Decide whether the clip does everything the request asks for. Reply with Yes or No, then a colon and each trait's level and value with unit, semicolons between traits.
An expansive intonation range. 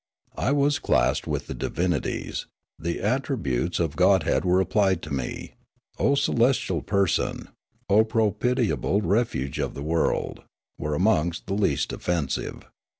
Yes: wide, 5.8 semitones